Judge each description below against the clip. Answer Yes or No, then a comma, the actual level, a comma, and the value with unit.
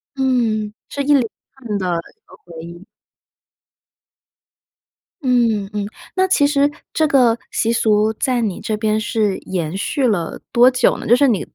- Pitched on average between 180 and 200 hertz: No, high, 225 Hz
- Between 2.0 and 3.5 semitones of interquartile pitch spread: No, average, 4.1 semitones